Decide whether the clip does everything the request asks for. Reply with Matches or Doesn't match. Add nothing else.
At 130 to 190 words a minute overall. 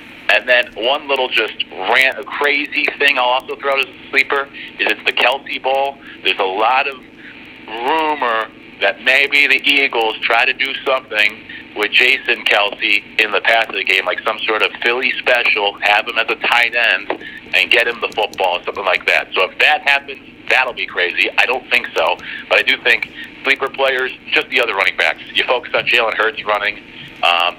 Doesn't match